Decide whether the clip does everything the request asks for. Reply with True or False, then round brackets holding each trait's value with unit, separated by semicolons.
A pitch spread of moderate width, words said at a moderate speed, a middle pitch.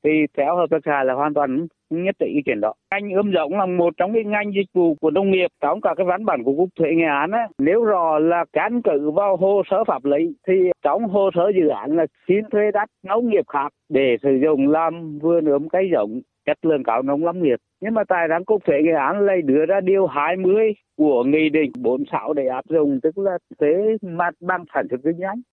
True (4.3 semitones; 240 wpm; 170 Hz)